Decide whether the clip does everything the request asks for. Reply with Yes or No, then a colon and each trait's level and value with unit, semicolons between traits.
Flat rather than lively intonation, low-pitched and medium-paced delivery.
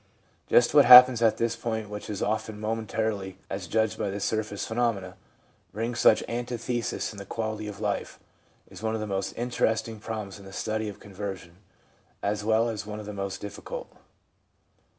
Yes: narrow, 1.9 semitones; low, 110 Hz; average, 170 wpm